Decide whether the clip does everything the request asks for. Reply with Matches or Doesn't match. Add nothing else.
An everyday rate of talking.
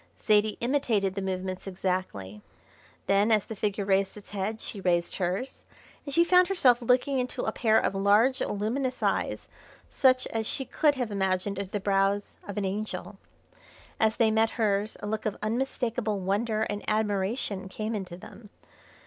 Matches